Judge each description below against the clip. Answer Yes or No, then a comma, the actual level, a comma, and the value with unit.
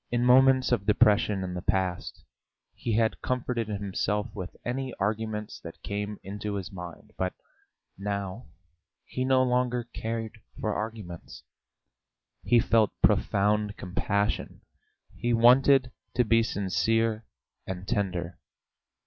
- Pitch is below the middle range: Yes, low, 105 Hz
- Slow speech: Yes, slow, 120 wpm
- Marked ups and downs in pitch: No, average, 3.4 semitones